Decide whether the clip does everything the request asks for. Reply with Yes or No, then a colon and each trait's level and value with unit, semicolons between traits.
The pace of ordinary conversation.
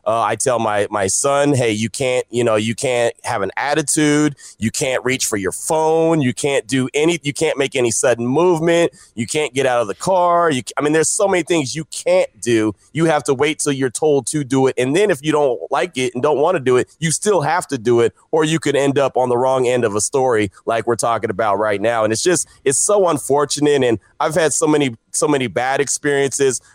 No: fast, 250 wpm